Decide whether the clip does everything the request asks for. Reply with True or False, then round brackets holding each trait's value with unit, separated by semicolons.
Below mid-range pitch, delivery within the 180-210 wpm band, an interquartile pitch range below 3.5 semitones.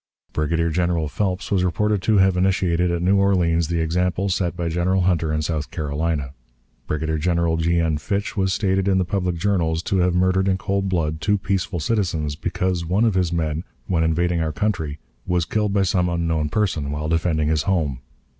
True (85 Hz; 190 wpm; 2.8 semitones)